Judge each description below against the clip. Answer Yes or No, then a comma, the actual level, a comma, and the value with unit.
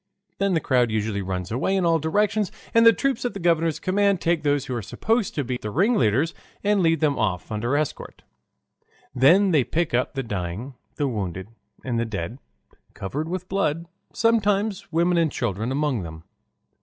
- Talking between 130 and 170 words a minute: No, average, 180 wpm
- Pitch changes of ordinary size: No, wide, 8.4 semitones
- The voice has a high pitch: No, medium, 150 Hz